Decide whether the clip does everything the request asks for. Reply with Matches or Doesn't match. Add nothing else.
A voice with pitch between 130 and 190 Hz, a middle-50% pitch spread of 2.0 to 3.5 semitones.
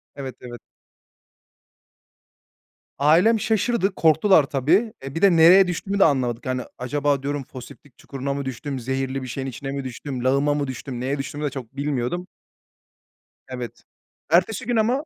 Doesn't match